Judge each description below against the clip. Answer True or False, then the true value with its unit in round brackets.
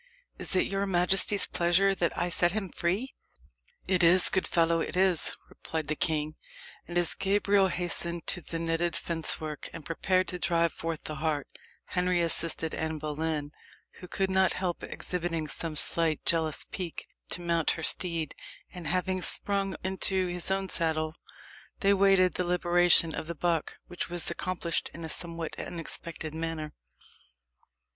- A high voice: False (170 Hz)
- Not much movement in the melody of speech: True (2.2 semitones)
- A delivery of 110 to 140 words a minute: False (155 wpm)